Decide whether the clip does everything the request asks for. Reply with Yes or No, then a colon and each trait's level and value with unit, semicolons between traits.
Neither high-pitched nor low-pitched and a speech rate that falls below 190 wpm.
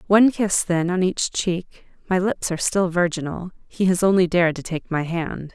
No: medium, 180 Hz; average, 195 wpm